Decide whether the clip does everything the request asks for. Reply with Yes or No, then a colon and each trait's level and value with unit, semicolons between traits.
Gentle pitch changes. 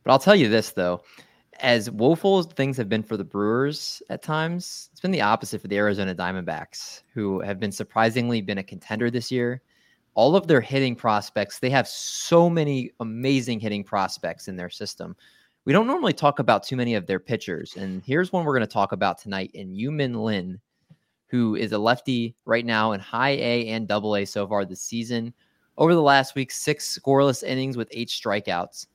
No: average, 4.9 semitones